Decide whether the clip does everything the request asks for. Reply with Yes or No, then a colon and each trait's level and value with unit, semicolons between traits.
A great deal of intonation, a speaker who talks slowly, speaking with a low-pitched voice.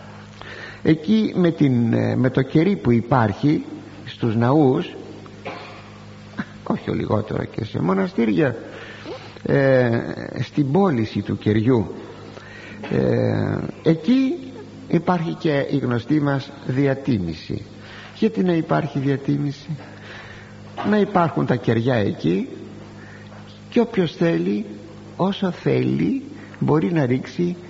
Yes: wide, 7.6 semitones; slow, 100 wpm; low, 130 Hz